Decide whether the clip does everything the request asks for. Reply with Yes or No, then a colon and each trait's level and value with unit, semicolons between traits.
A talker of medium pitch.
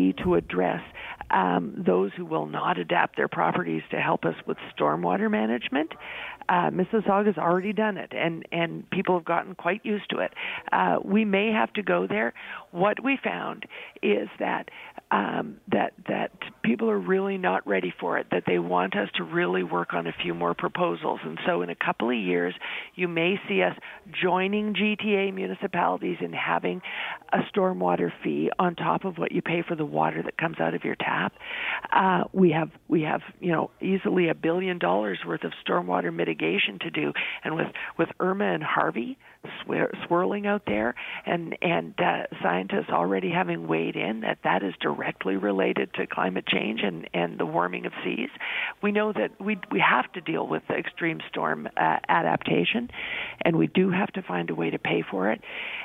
Yes: medium, 180 Hz